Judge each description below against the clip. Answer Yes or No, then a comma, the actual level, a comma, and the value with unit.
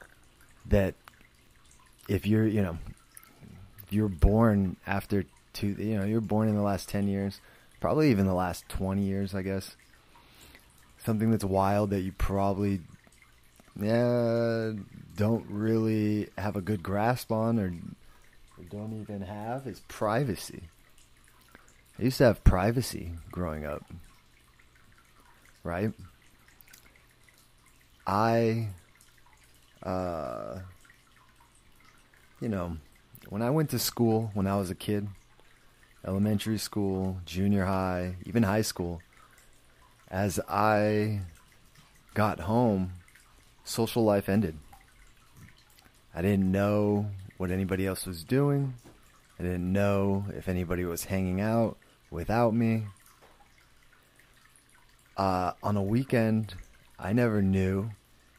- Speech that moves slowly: Yes, slow, 110 wpm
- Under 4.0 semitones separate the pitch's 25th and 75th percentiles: Yes, average, 2.9 semitones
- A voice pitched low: Yes, low, 100 Hz